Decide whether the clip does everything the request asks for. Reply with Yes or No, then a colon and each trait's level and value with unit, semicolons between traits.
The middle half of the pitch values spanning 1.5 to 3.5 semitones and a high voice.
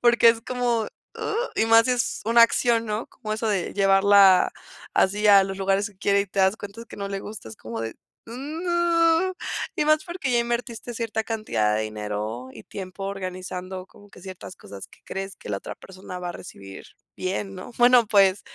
No: average, 4.2 semitones; high, 200 Hz